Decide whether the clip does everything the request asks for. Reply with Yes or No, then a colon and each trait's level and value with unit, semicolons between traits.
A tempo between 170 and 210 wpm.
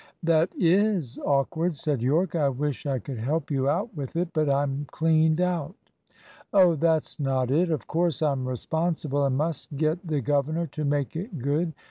Yes: average, 175 wpm